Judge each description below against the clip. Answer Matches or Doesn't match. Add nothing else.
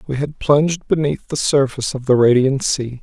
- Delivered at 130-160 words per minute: Doesn't match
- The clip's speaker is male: Matches